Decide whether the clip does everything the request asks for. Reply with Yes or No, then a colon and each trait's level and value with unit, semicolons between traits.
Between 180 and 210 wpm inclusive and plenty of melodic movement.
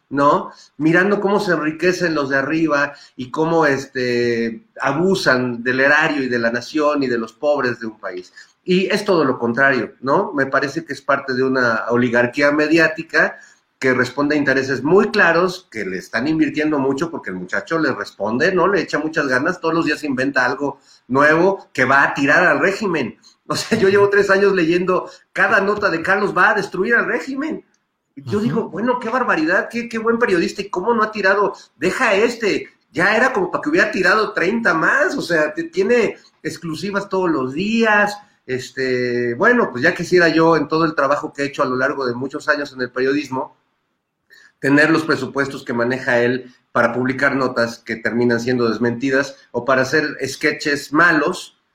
Yes: fast, 190 wpm; wide, 6.6 semitones